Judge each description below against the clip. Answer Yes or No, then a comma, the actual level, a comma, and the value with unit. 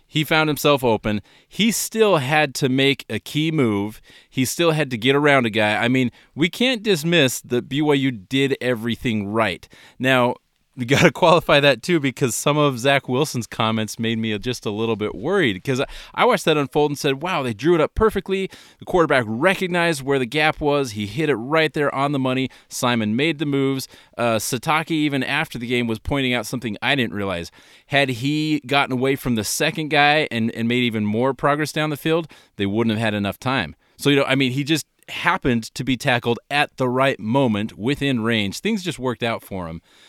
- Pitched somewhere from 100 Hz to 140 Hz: Yes, low, 135 Hz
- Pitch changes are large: No, average, 4.5 semitones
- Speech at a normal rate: No, fast, 210 wpm